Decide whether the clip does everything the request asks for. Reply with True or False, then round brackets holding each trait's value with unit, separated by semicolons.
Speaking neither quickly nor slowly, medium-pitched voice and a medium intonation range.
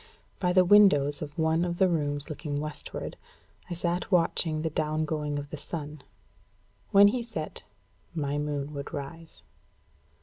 True (155 wpm; 155 Hz; 3.0 semitones)